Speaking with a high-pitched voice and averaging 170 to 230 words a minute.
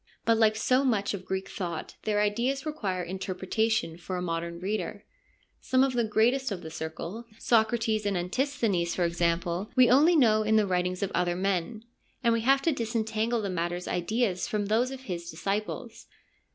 Yes: high, 210 Hz; average, 180 wpm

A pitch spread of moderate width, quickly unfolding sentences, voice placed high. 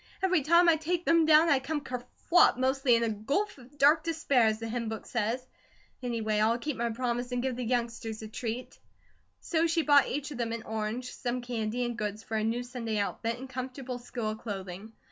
Yes: average, 3.9 semitones; fast, 210 wpm; high, 245 Hz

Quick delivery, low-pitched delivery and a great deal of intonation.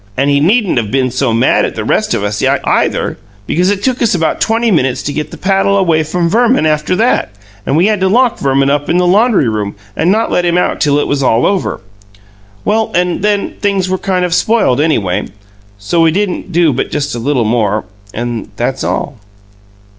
No: fast, 215 wpm; medium, 165 Hz; wide, 6.6 semitones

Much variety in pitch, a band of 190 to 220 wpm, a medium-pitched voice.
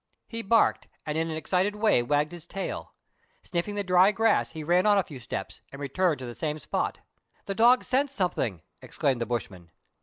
Yes: wide, 6.8 semitones; fast, 205 wpm; medium, 175 Hz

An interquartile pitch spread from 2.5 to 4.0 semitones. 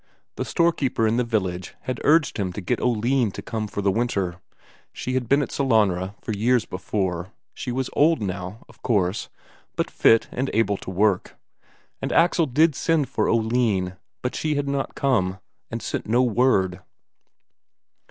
No: average, 5.1 semitones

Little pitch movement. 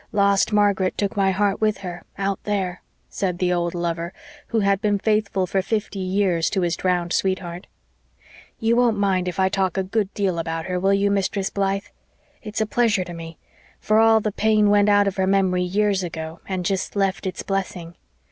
Yes: narrow, 2.1 semitones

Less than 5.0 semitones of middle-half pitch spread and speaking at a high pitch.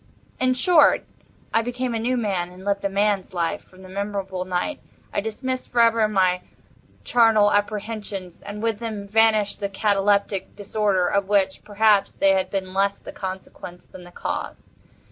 Yes: narrow, 2.6 semitones; high, 205 Hz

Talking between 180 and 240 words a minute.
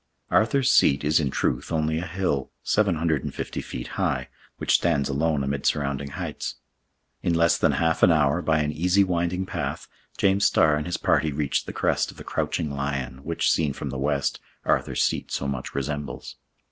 Yes: average, 190 wpm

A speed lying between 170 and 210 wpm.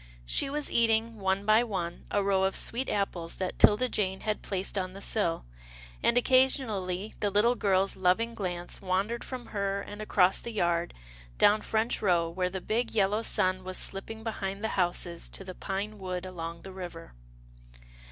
Yes: average, 175 wpm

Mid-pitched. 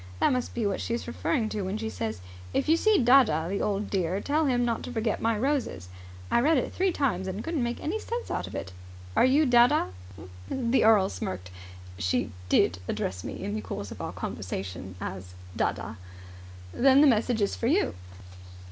No: high, 225 Hz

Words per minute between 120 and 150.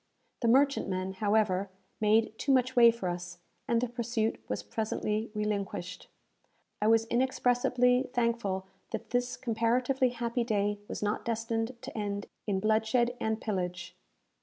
Yes: slow, 135 wpm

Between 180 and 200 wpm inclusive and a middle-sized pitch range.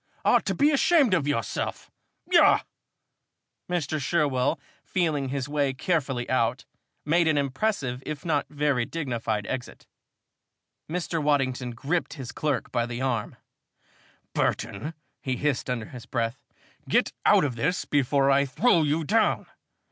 No: slow, 135 wpm; average, 4.2 semitones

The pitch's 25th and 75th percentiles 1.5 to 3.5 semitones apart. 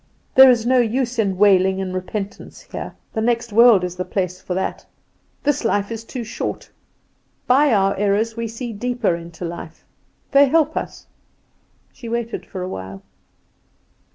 No: average, 4.3 semitones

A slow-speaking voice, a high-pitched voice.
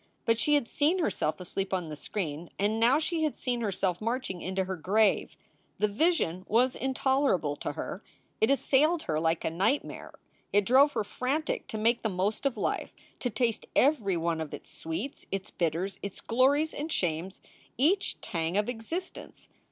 No: average, 175 wpm; high, 220 Hz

